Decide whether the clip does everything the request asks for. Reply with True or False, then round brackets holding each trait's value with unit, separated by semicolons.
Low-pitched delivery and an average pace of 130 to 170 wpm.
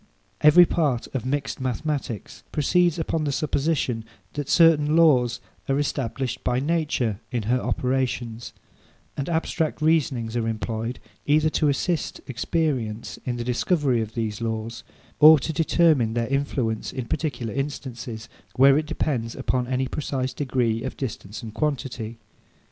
True (130 Hz; 140 wpm)